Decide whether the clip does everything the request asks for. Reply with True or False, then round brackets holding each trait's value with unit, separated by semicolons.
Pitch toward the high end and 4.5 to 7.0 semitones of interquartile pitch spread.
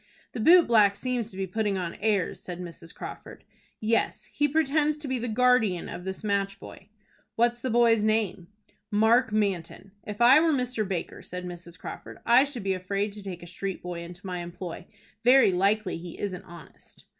True (205 Hz; 4.8 semitones)